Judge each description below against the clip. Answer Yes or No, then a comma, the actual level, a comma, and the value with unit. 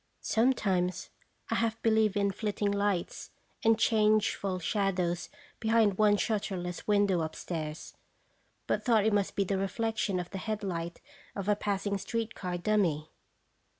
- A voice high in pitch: Yes, high, 200 Hz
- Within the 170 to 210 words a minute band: No, slow, 135 wpm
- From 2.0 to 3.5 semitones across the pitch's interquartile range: Yes, average, 2.8 semitones